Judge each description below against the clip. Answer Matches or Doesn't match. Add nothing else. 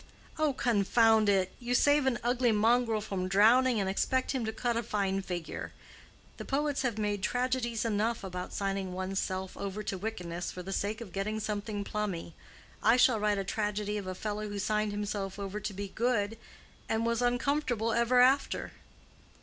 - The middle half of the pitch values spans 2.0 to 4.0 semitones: Matches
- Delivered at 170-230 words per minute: Matches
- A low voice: Doesn't match